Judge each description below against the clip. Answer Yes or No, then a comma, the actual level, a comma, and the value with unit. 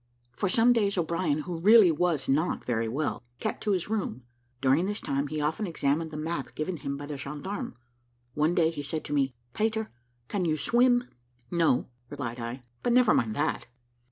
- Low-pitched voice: No, medium, 155 Hz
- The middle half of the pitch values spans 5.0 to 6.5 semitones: Yes, wide, 5.6 semitones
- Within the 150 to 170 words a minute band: No, average, 185 wpm